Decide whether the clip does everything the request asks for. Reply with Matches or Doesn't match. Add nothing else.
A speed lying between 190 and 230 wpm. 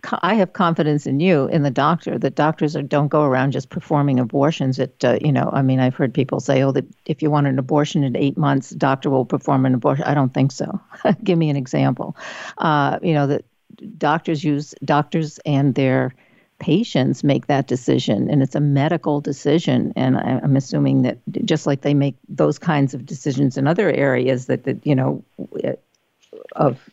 Matches